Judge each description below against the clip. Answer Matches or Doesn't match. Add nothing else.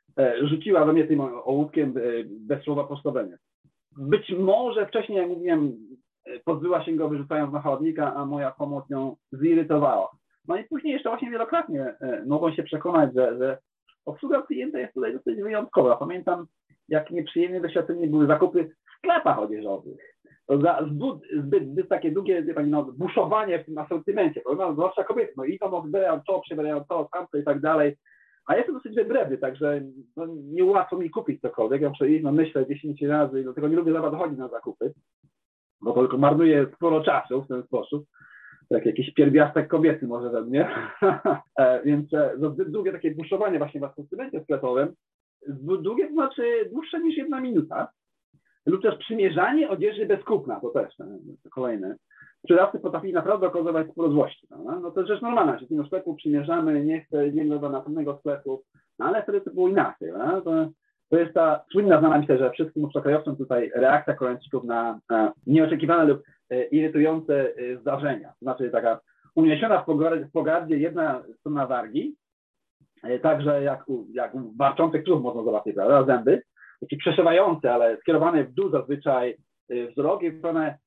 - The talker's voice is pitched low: Doesn't match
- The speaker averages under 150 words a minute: Doesn't match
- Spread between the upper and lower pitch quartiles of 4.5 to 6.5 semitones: Matches